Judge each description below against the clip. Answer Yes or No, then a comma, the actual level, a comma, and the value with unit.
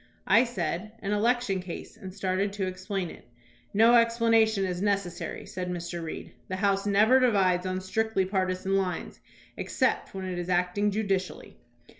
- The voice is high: Yes, high, 195 Hz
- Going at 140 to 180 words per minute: Yes, average, 155 wpm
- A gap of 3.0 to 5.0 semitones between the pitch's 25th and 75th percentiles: No, narrow, 2.5 semitones